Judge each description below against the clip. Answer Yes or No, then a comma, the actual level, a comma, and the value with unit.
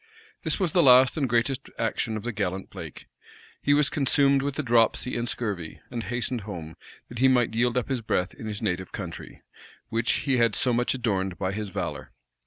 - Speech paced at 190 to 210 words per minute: Yes, average, 200 wpm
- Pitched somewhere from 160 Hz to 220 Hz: No, low, 120 Hz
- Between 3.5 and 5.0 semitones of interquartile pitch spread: Yes, average, 3.8 semitones